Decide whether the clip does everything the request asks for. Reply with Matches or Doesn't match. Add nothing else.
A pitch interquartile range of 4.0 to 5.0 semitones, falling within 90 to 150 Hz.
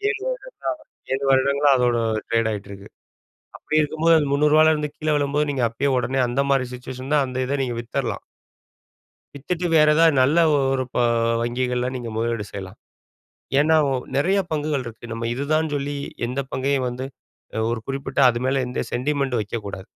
Doesn't match